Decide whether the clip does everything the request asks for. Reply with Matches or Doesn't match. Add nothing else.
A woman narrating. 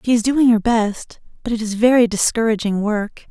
Matches